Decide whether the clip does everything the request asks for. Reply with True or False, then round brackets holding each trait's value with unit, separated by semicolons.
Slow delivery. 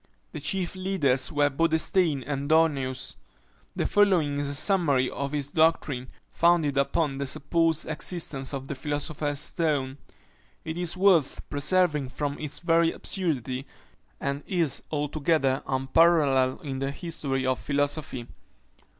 True (130 wpm)